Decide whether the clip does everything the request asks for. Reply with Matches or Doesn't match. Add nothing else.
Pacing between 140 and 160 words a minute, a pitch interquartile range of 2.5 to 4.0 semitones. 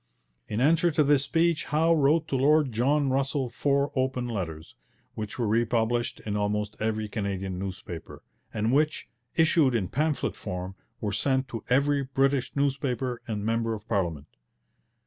Doesn't match